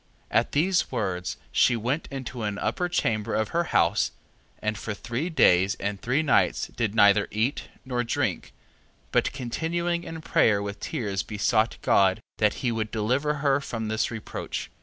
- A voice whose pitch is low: Yes, low, 115 Hz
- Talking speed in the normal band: Yes, average, 165 wpm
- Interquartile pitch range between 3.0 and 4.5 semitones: No, average, 5.0 semitones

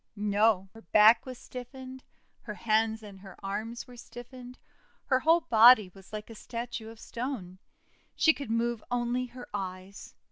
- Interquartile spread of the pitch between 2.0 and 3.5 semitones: Yes, average, 2.9 semitones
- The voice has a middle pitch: No, high, 230 Hz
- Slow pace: No, average, 155 wpm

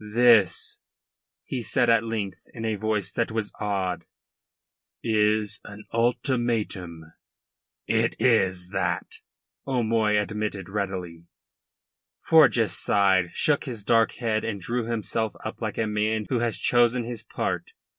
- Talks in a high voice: No, low, 110 Hz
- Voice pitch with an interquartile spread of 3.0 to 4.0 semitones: No, narrow, 2.4 semitones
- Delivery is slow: Yes, slow, 125 wpm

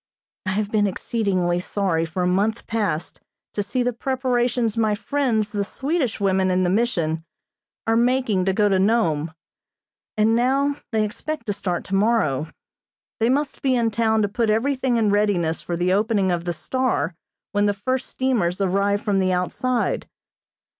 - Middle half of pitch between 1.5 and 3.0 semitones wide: No, average, 4.2 semitones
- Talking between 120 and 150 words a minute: No, average, 165 wpm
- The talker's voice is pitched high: Yes, high, 210 Hz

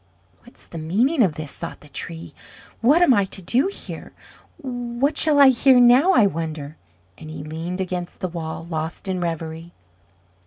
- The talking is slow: No, average, 170 wpm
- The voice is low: No, medium, 180 Hz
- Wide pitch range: Yes, wide, 7.6 semitones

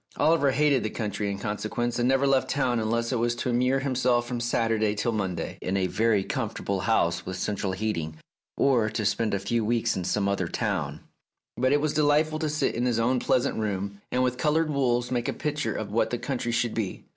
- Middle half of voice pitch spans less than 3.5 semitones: No, average, 3.8 semitones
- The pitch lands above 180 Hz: No, low, 115 Hz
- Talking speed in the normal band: No, fast, 215 wpm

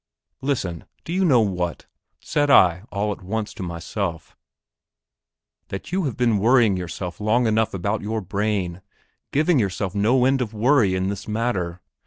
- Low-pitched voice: Yes, low, 105 Hz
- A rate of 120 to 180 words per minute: Yes, average, 160 wpm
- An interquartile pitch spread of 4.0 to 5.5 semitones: Yes, average, 4.7 semitones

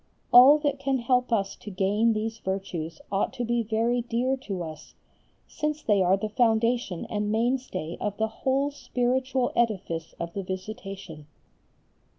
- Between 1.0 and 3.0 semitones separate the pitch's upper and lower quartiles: No, average, 4.3 semitones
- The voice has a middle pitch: No, high, 220 Hz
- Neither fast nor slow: Yes, average, 155 wpm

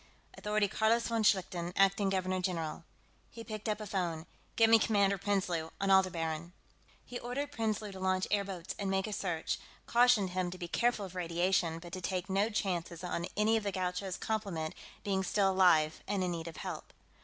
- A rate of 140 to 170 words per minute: No, average, 190 wpm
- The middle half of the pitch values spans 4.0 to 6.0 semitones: No, average, 2.9 semitones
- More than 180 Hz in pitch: Yes, high, 190 Hz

